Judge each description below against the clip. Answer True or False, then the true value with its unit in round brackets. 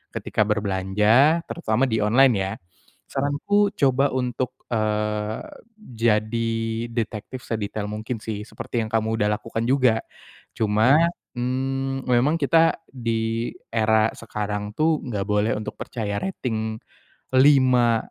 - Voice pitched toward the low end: True (115 Hz)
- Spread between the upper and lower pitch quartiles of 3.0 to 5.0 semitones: True (3.5 semitones)